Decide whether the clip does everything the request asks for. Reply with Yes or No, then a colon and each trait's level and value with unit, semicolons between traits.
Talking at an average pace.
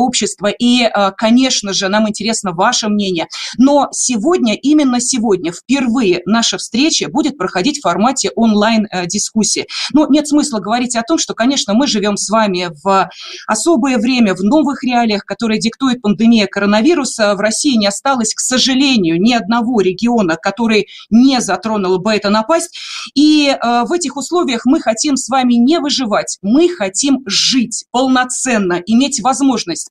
Yes: average, 145 wpm